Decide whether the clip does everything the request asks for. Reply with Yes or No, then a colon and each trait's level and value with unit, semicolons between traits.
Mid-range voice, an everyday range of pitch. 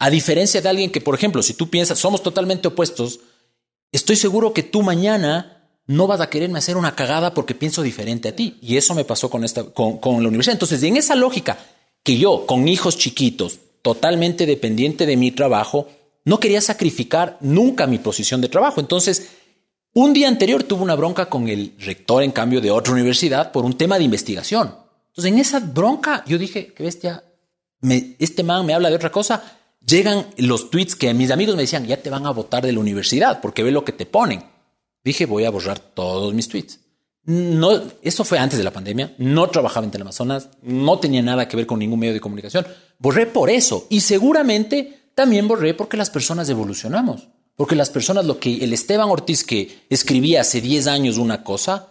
No: medium, 160 Hz; wide, 7.2 semitones